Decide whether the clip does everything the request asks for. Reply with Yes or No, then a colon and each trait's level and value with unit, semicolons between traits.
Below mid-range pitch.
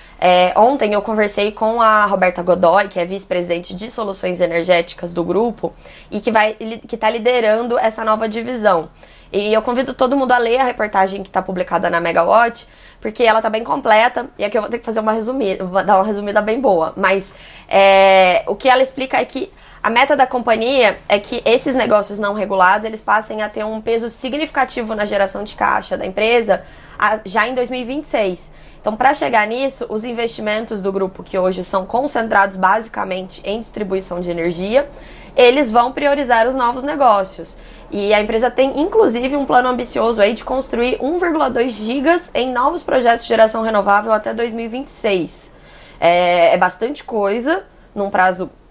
No: high, 220 Hz